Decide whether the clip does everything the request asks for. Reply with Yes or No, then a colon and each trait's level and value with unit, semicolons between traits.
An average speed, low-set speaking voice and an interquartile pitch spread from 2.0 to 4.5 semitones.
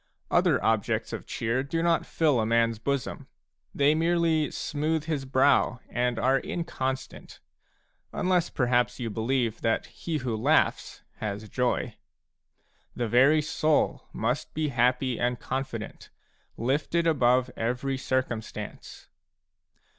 No: slow, 125 wpm; low, 130 Hz; average, 4.0 semitones